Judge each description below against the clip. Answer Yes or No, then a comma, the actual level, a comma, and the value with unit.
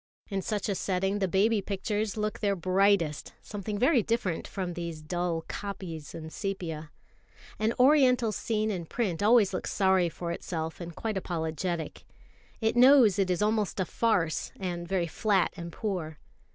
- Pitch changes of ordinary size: Yes, average, 3.8 semitones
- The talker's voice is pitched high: Yes, high, 195 Hz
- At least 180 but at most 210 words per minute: No, average, 160 wpm